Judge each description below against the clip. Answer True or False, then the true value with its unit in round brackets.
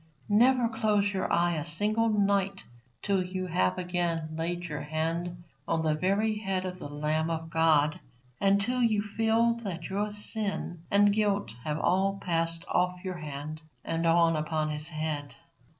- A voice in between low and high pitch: True (175 Hz)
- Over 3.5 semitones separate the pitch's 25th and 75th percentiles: True (3.9 semitones)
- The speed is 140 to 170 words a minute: True (165 wpm)